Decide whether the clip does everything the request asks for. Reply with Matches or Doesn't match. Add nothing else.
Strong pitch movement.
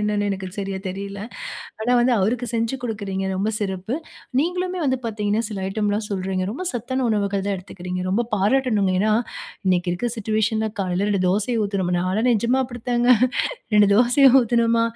Doesn't match